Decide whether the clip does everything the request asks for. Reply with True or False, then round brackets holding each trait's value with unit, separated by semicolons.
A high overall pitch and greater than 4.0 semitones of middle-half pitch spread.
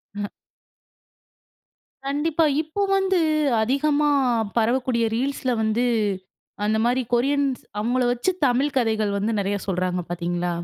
True (245 Hz; 4.9 semitones)